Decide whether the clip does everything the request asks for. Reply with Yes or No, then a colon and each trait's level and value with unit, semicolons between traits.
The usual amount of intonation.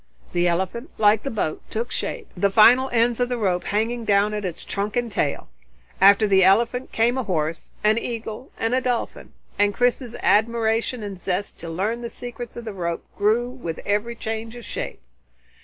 Yes: average, 3.2 semitones